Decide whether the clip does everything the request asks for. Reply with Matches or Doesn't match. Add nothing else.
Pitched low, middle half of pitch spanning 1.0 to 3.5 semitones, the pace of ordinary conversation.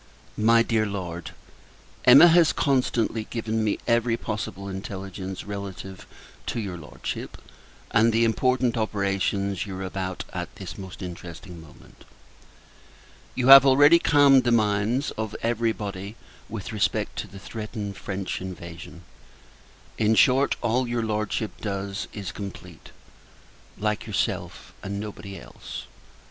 Doesn't match